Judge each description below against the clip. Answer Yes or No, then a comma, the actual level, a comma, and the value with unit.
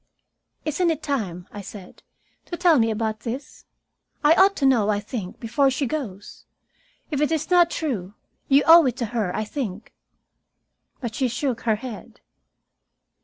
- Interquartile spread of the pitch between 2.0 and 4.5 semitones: No, wide, 5.6 semitones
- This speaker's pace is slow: No, average, 165 wpm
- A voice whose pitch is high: Yes, high, 245 Hz